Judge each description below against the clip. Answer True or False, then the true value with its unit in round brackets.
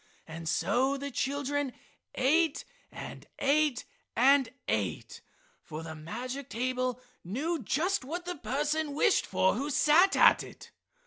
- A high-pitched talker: True (275 Hz)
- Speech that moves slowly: True (130 wpm)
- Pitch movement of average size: True (3.6 semitones)